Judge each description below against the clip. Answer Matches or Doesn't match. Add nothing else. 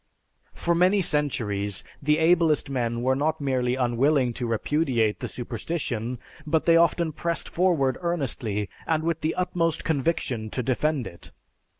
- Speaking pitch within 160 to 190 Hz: Doesn't match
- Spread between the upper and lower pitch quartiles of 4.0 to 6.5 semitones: Matches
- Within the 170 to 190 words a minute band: Doesn't match